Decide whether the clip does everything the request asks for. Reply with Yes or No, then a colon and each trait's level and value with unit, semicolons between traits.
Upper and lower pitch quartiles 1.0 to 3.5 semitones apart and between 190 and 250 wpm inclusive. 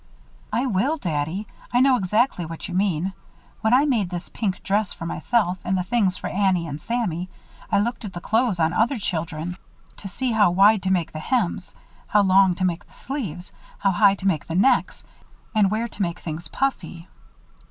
No: average, 4.0 semitones; average, 195 wpm